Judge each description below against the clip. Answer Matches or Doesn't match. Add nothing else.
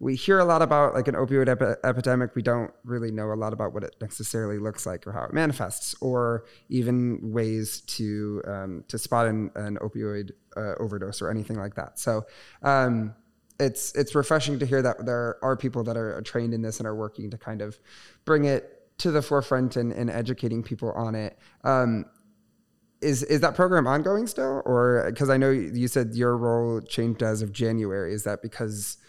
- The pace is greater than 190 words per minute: Matches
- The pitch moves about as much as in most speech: Matches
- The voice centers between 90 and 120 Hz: Matches